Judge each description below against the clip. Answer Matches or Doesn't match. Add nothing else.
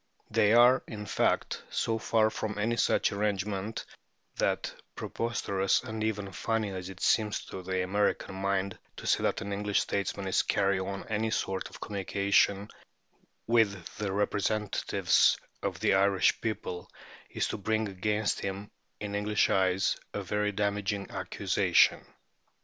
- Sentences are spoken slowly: Doesn't match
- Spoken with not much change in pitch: Matches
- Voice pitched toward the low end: Matches